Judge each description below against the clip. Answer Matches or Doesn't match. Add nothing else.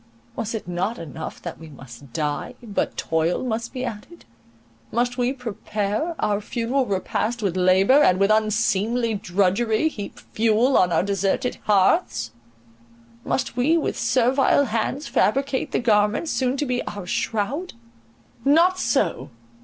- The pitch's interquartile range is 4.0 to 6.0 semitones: Matches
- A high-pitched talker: Matches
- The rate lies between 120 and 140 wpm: Matches